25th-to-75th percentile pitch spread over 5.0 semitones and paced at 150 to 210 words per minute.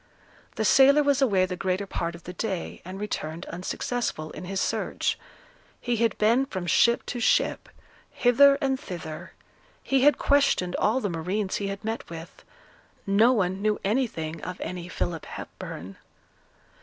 Yes: wide, 5.4 semitones; average, 155 wpm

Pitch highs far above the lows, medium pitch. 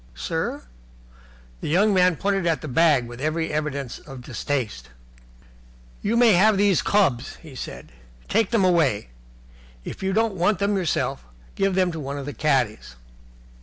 Yes: wide, 6.2 semitones; medium, 165 Hz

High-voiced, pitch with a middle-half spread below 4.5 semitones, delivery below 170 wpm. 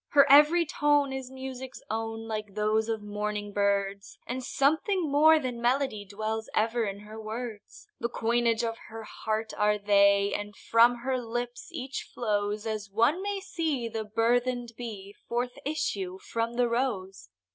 Yes: high, 230 Hz; average, 3.5 semitones; average, 155 wpm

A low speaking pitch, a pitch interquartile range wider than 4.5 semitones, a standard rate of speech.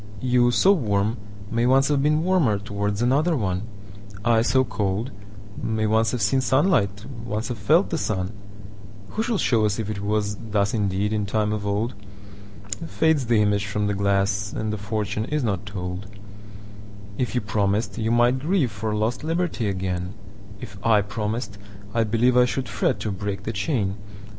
No: low, 105 Hz; average, 3.0 semitones; average, 150 wpm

